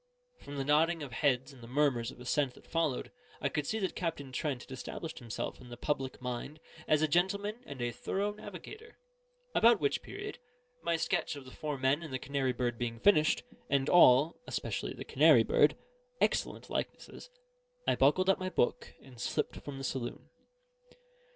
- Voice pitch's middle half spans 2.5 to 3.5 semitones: No, average, 4.9 semitones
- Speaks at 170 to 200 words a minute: Yes, average, 185 wpm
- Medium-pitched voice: Yes, medium, 145 Hz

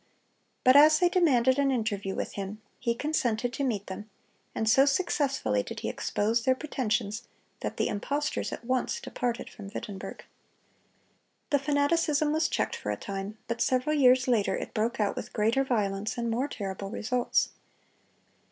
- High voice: Yes, high, 245 Hz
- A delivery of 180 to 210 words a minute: No, average, 160 wpm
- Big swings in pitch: No, average, 4.8 semitones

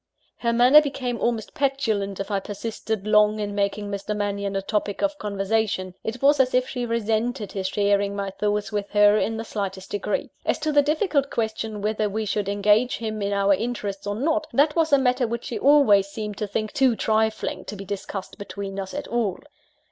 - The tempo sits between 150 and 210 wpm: Yes, average, 200 wpm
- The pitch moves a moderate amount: Yes, average, 3.3 semitones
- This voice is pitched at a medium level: No, high, 215 Hz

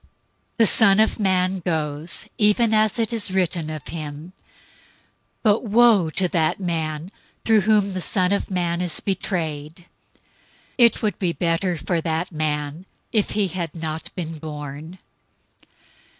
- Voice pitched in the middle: Yes, medium, 180 Hz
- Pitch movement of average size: Yes, average, 4.2 semitones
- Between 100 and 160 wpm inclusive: Yes, average, 145 wpm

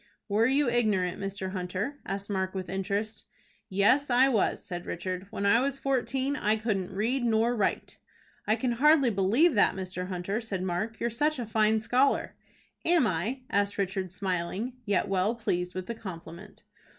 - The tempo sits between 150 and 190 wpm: Yes, average, 170 wpm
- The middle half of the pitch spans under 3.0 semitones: No, average, 4.2 semitones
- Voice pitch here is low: No, high, 210 Hz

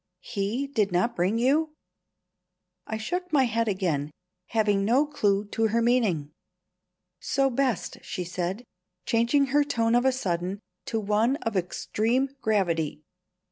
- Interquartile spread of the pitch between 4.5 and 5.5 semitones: Yes, average, 4.9 semitones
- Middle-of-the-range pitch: No, high, 225 Hz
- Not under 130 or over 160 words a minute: Yes, average, 140 wpm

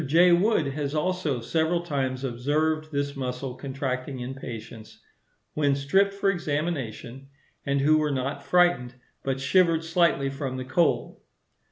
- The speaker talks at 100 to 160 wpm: Yes, average, 140 wpm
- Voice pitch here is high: No, medium, 140 Hz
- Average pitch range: Yes, average, 3.8 semitones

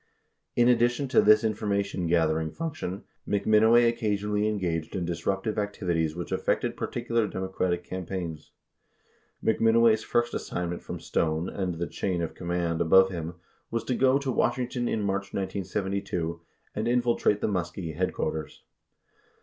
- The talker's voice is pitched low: Yes, low, 100 Hz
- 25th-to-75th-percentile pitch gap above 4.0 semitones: Yes, average, 4.4 semitones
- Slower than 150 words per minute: Yes, average, 140 wpm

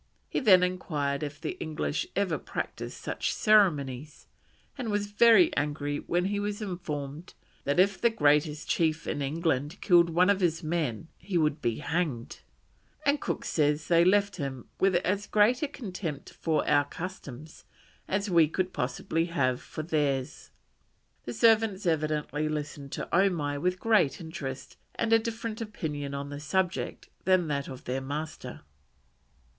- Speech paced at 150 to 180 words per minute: Yes, average, 155 wpm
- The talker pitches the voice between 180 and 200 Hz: No, medium, 165 Hz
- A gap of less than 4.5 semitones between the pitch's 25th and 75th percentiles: No, average, 4.8 semitones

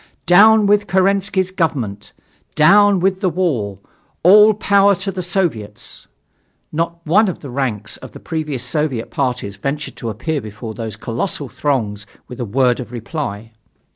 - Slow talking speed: No, average, 150 wpm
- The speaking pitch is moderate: Yes, medium, 150 Hz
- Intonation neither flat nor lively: No, wide, 8.2 semitones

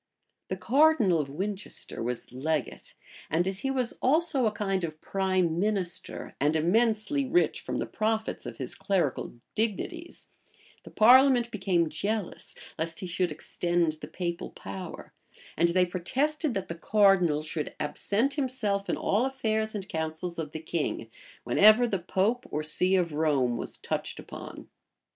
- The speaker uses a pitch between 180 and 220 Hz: Yes, high, 190 Hz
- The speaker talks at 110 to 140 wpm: No, average, 155 wpm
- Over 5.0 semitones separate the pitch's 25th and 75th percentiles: Yes, wide, 5.6 semitones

